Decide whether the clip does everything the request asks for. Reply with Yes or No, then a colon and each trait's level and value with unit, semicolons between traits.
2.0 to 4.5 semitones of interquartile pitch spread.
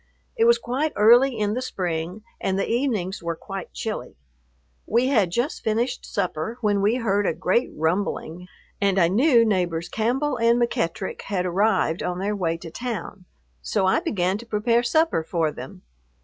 No: average, 4.9 semitones